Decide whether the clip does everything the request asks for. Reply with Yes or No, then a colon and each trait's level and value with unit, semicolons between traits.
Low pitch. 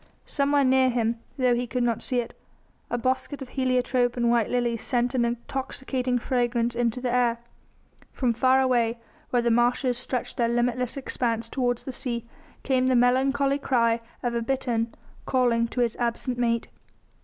No: high, 245 Hz